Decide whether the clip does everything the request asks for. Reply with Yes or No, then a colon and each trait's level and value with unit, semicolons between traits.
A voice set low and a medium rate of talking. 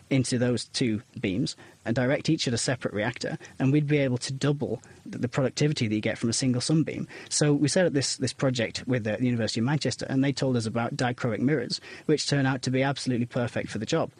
No: low, 130 Hz; fast, 235 wpm